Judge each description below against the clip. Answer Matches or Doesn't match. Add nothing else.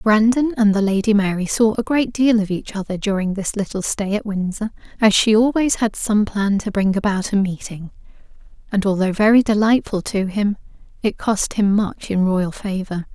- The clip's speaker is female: Matches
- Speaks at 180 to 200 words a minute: Matches